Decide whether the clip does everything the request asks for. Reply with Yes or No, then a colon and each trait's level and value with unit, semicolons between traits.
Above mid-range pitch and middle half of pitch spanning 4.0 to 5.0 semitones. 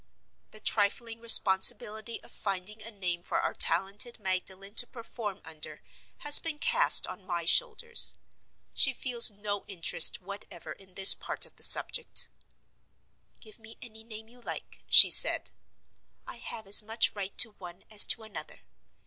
No: high, 210 Hz; average, 3.3 semitones